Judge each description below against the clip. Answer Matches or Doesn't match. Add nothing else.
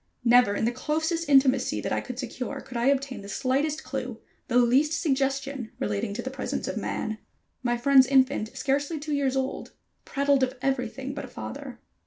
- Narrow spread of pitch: Matches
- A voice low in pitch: Doesn't match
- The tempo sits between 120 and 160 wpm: Doesn't match